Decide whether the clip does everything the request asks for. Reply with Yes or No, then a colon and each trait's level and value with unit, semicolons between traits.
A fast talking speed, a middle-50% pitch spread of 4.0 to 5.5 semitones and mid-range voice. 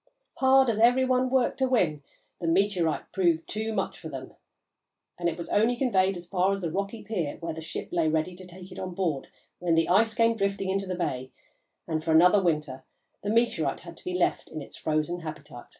Yes: fast, 215 wpm; average, 4.5 semitones; medium, 180 Hz